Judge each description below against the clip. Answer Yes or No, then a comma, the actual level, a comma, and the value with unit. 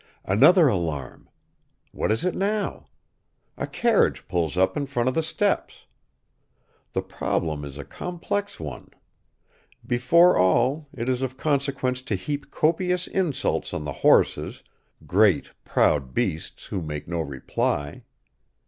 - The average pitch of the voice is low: Yes, low, 125 Hz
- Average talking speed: No, slow, 130 wpm